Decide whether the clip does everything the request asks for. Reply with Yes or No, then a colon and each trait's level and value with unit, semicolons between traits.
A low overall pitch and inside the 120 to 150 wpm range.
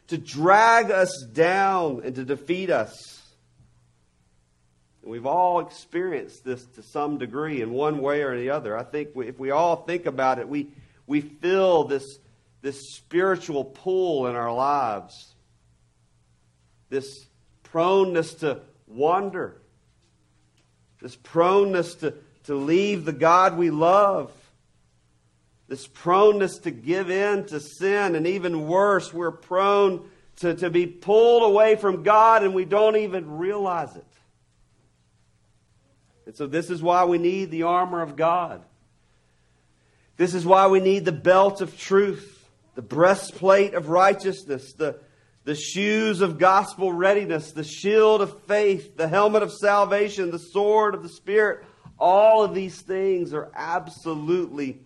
No: medium, 170 Hz; average, 140 wpm